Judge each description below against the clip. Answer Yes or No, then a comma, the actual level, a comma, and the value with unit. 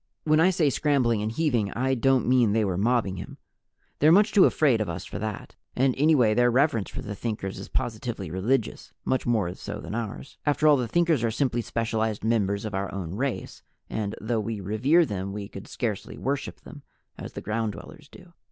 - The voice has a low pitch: Yes, low, 115 Hz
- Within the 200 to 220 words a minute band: Yes, fast, 205 wpm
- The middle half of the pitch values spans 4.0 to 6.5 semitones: Yes, average, 4.7 semitones